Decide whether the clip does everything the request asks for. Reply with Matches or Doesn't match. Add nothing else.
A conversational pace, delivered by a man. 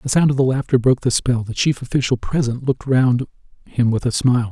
Doesn't match